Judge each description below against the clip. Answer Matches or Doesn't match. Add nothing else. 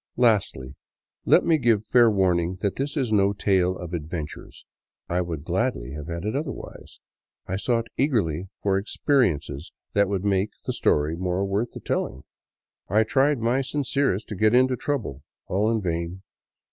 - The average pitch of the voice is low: Matches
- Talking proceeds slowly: Doesn't match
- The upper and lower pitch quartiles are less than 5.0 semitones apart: Doesn't match